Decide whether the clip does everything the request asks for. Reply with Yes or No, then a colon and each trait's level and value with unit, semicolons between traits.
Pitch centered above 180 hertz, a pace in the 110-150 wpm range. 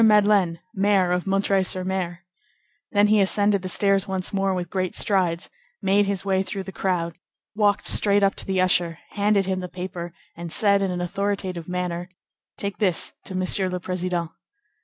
No: high, 190 Hz; average, 180 wpm